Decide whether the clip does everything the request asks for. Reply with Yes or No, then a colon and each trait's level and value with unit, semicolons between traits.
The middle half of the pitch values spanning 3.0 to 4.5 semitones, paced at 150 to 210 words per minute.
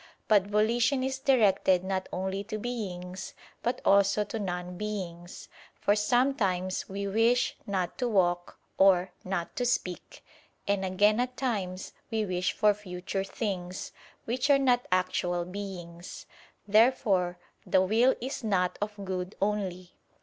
No: average, 3.4 semitones; slow, 135 wpm